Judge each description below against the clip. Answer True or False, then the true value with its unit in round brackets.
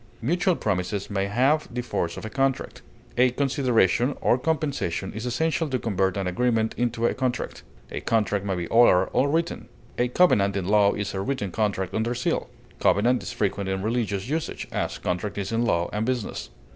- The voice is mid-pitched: False (115 Hz)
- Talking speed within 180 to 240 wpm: True (185 wpm)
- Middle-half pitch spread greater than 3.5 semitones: True (4.4 semitones)